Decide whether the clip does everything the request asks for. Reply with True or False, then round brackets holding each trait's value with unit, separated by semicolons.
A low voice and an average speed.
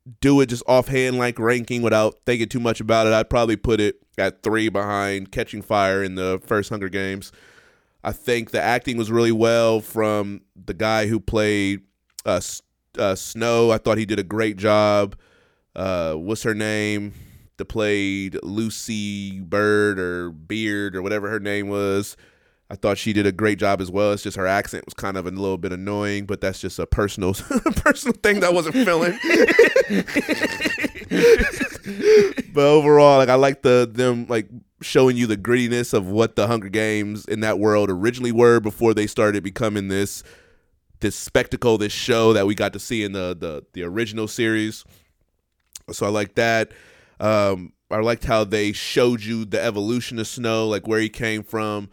True (110 Hz; 180 wpm)